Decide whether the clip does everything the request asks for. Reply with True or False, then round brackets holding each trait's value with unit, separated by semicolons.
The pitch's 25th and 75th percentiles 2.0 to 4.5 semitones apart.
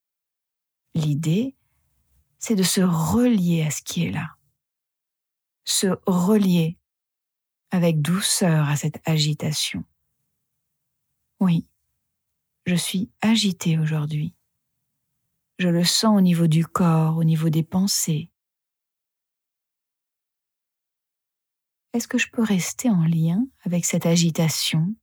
True (3.4 semitones)